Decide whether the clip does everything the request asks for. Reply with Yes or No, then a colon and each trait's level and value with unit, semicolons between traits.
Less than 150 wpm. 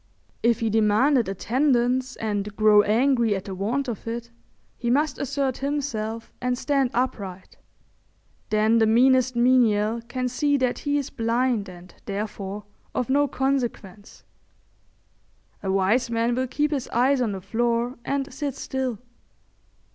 Yes: average, 140 wpm